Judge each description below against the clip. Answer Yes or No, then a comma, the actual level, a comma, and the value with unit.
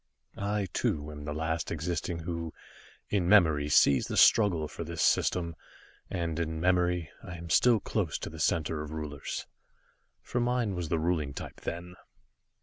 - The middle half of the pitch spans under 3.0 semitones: Yes, narrow, 2.4 semitones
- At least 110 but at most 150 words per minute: No, average, 160 wpm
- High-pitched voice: No, very low, 85 Hz